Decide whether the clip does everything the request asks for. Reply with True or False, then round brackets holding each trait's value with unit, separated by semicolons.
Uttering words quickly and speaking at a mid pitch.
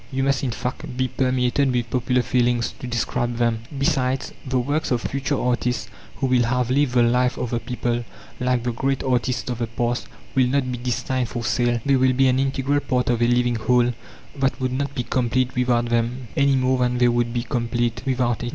False (215 wpm; 125 Hz)